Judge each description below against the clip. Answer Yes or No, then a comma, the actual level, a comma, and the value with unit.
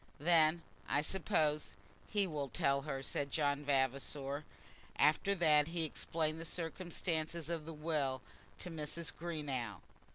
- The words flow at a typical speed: No, slow, 130 wpm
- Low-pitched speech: No, medium, 155 Hz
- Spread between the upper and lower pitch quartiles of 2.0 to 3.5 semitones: Yes, average, 2.7 semitones